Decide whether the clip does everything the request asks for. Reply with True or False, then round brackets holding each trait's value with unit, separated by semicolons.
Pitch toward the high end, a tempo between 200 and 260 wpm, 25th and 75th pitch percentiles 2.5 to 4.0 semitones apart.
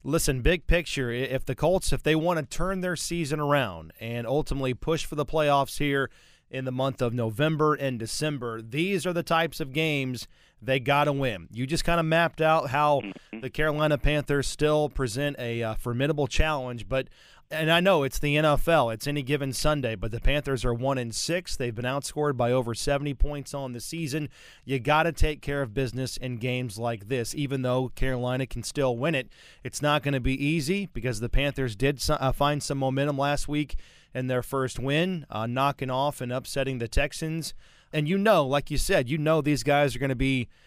False (140 Hz; 205 wpm; 3.0 semitones)